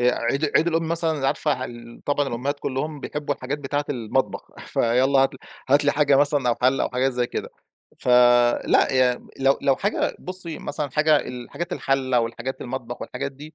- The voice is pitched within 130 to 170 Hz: Yes, low, 135 Hz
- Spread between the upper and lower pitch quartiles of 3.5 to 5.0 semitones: No, average, 2.9 semitones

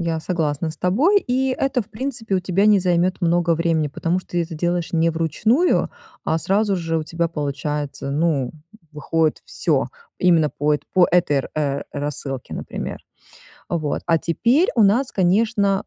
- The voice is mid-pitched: Yes, medium, 170 Hz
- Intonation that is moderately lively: Yes, average, 4.2 semitones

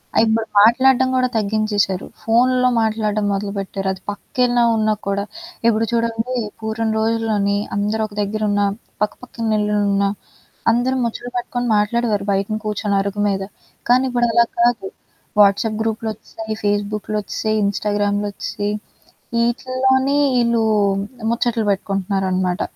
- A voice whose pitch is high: Yes, high, 215 Hz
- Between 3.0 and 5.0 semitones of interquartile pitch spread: No, narrow, 2.5 semitones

